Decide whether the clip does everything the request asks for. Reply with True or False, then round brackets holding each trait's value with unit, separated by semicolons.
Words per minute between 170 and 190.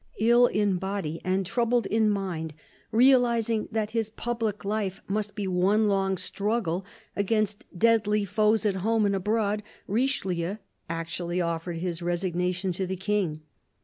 False (140 wpm)